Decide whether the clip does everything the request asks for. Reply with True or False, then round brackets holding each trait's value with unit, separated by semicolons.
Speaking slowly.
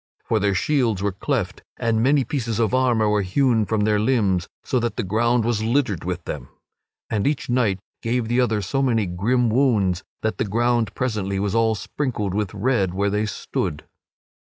False (185 wpm)